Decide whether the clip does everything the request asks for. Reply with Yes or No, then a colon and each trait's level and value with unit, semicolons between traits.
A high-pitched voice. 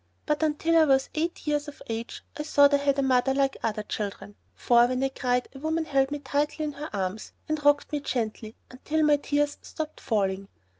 Yes: very high, 280 Hz